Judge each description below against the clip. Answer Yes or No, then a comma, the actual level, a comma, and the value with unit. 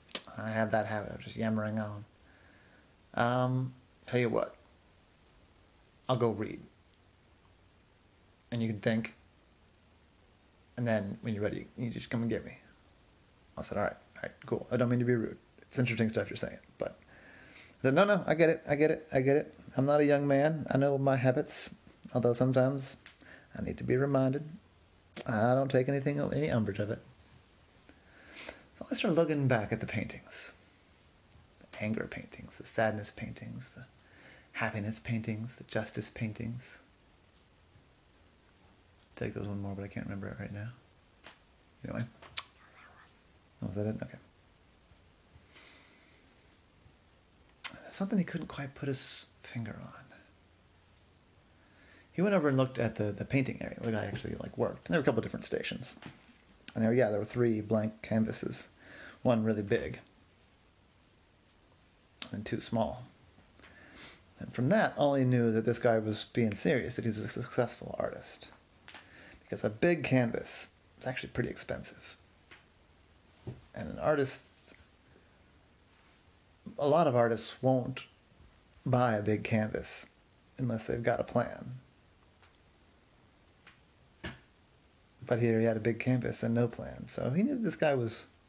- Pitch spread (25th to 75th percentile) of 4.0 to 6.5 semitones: Yes, average, 4.8 semitones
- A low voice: Yes, low, 110 Hz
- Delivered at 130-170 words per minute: Yes, average, 150 wpm